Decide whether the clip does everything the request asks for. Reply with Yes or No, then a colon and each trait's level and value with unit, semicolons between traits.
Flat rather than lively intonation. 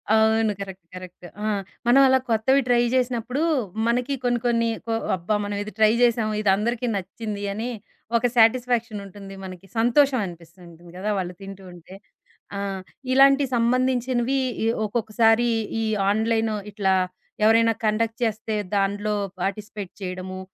No: average, 3.4 semitones